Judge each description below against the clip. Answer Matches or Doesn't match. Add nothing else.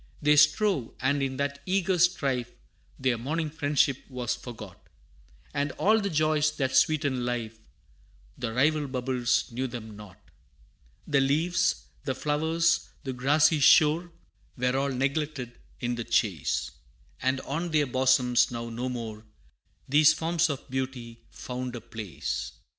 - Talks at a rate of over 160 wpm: Doesn't match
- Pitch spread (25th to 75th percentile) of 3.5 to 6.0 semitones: Matches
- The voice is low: Matches